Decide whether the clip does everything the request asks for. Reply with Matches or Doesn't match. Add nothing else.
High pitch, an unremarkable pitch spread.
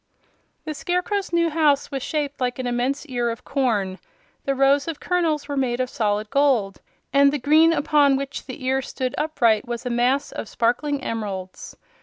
Matches